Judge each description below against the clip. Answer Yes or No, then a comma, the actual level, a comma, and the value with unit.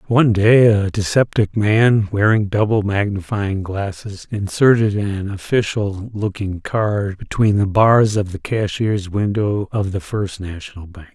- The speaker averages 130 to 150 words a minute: Yes, average, 140 wpm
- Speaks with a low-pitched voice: Yes, low, 100 Hz